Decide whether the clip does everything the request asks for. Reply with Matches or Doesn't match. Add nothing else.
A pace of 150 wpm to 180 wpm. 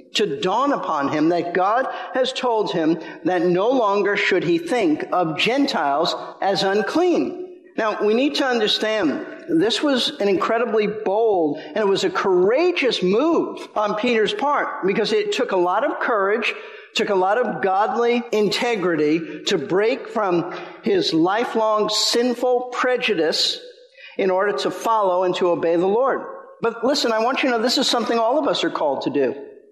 Matches